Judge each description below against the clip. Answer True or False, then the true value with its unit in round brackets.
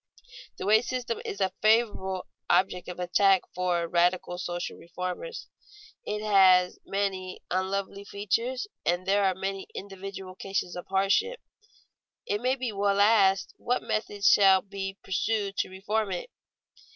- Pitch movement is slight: True (1.9 semitones)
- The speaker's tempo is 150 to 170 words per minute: False (140 wpm)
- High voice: True (195 Hz)